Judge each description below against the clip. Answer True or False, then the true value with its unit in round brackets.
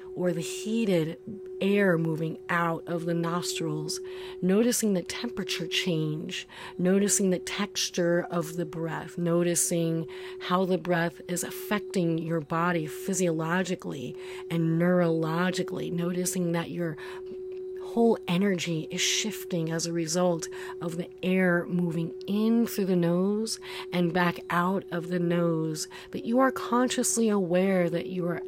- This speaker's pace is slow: True (130 wpm)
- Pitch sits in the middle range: True (180 Hz)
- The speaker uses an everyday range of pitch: False (1.5 semitones)